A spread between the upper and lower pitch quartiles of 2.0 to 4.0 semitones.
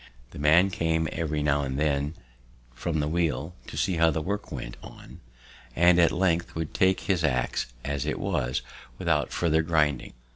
Yes: average, 2.7 semitones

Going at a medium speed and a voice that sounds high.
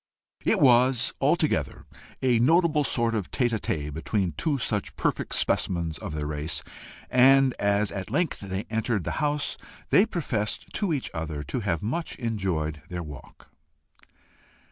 No: average, 150 wpm; low, 110 Hz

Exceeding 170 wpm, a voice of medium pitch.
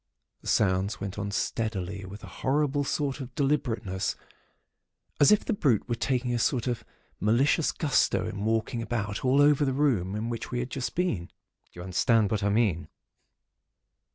No: average, 180 wpm; low, 115 Hz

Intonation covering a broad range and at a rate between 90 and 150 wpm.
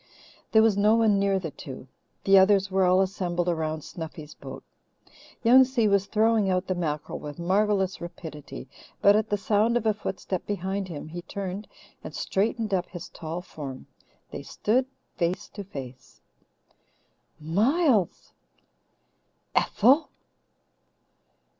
No: average, 3.6 semitones; slow, 135 wpm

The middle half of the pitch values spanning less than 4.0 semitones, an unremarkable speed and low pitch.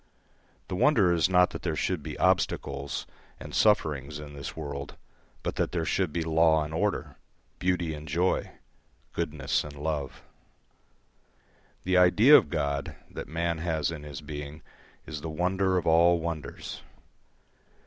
Yes: average, 3.1 semitones; average, 150 wpm; very low, 80 Hz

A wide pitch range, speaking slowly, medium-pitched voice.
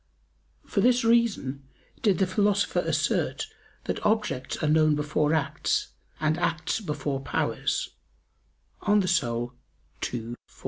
Yes: wide, 6.6 semitones; slow, 120 wpm; medium, 155 Hz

